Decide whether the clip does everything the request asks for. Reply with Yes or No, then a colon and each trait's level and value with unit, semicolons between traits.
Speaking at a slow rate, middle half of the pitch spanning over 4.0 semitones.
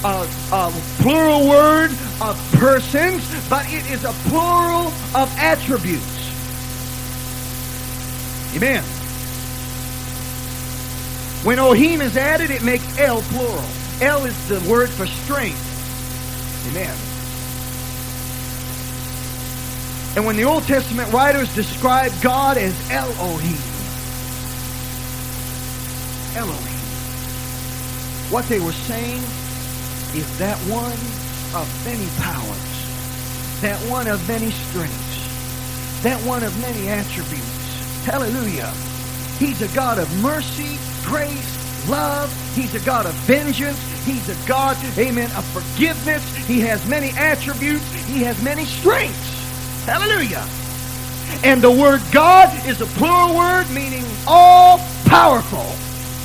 Yes: slow, 105 wpm; wide, 5.5 semitones